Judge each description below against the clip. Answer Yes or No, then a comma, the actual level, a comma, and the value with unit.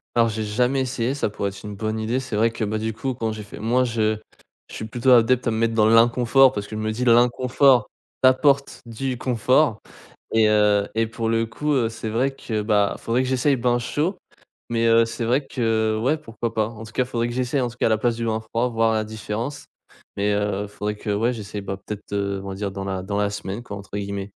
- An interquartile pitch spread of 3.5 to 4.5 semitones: No, average, 2.7 semitones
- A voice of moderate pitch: No, low, 115 Hz